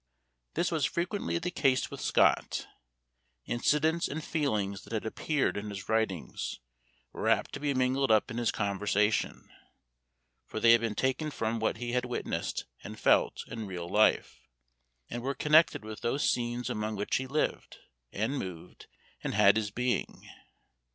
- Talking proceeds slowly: No, average, 160 wpm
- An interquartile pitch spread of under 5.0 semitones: Yes, average, 4.5 semitones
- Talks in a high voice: No, low, 120 Hz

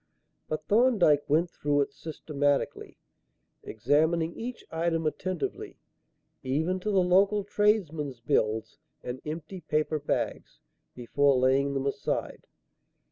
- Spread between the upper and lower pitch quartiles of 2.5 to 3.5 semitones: No, average, 4.3 semitones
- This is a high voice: No, medium, 155 Hz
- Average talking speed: No, slow, 110 wpm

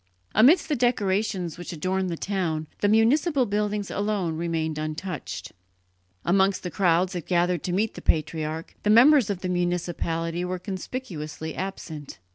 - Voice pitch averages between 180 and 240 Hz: Yes, medium, 185 Hz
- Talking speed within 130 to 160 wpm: Yes, average, 145 wpm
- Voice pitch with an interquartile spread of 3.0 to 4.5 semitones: Yes, average, 3.8 semitones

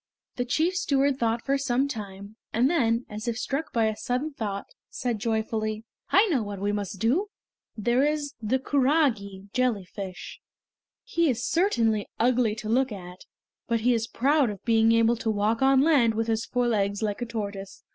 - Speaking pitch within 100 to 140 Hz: No, high, 230 Hz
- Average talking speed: Yes, average, 180 wpm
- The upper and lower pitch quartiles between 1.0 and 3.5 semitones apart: No, average, 3.9 semitones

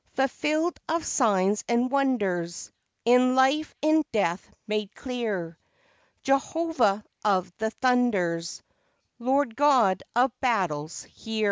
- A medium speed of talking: No, slow, 105 wpm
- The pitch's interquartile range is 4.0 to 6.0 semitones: Yes, wide, 5.6 semitones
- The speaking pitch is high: Yes, high, 235 Hz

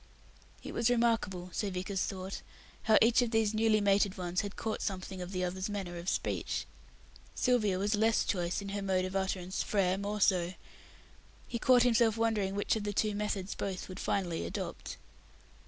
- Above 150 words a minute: Yes, average, 180 wpm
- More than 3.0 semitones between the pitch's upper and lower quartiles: No, average, 2.7 semitones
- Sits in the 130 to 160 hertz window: No, high, 200 Hz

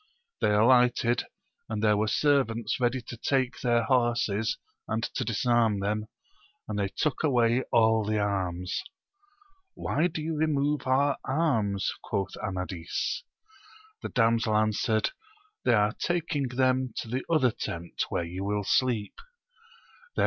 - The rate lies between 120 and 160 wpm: Yes, average, 140 wpm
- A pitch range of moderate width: Yes, average, 3.8 semitones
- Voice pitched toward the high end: No, low, 115 Hz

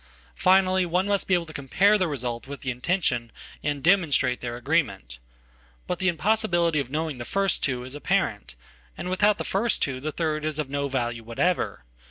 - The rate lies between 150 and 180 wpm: No, average, 190 wpm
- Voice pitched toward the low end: No, medium, 155 Hz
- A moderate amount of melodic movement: No, wide, 6.2 semitones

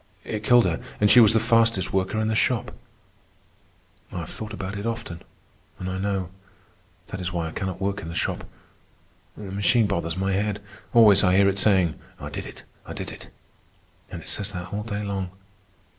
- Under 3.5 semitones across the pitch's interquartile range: Yes, narrow, 2.4 semitones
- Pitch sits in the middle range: No, low, 100 Hz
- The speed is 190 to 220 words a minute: Yes, average, 200 wpm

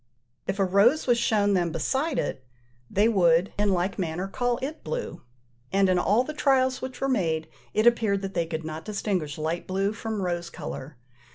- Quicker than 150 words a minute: Yes, average, 190 wpm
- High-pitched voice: Yes, high, 195 Hz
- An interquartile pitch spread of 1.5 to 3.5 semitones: No, wide, 5.5 semitones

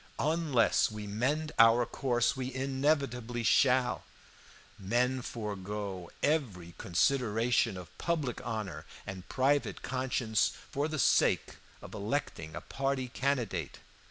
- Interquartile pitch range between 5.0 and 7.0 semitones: No, average, 4.5 semitones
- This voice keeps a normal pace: No, slow, 110 wpm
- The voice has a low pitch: Yes, low, 125 Hz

